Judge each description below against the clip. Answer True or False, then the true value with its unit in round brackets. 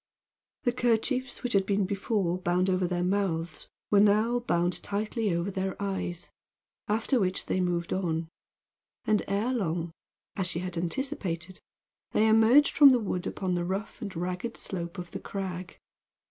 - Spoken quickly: False (160 wpm)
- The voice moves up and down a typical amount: True (3.6 semitones)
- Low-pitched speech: False (190 Hz)